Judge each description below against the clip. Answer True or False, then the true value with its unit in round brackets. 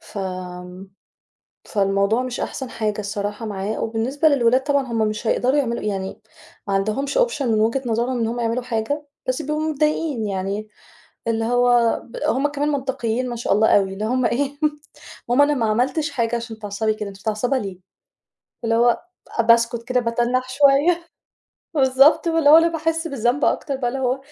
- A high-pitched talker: True (240 Hz)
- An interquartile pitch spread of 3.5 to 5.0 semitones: True (3.9 semitones)